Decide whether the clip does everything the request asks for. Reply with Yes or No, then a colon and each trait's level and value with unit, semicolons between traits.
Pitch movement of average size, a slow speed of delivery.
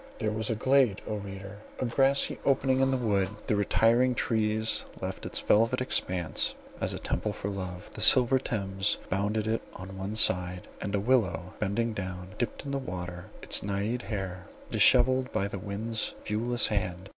No: average, 3.7 semitones; average, 175 wpm